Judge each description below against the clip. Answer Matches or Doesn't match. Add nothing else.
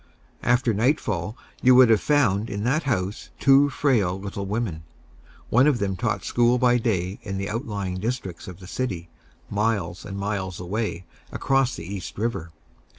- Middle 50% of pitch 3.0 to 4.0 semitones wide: Doesn't match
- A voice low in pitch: Matches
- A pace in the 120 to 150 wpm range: Doesn't match